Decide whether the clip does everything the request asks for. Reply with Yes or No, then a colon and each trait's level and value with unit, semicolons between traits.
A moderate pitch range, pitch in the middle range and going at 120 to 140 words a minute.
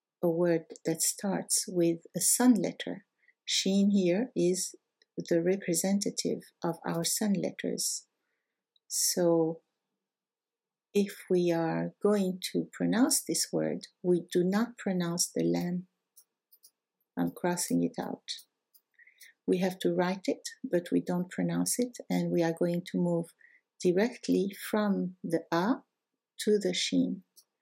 Yes: average, 3.5 semitones; medium, 180 Hz; average, 130 wpm